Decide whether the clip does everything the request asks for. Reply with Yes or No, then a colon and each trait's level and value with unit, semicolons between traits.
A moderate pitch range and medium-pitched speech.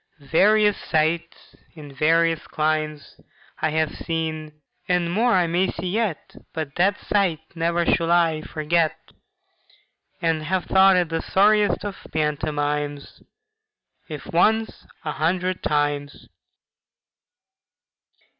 Yes: average, 3.0 semitones; medium, 165 Hz